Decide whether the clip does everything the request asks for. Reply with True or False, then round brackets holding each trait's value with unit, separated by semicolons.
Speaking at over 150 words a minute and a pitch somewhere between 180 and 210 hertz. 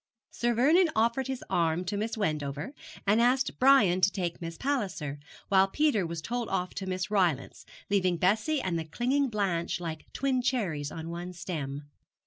True (170 wpm; 190 Hz)